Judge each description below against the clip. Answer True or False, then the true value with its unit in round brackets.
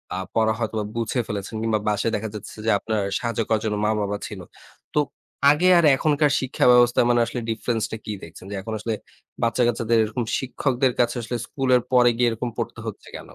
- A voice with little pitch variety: True (2.1 semitones)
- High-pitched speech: False (115 Hz)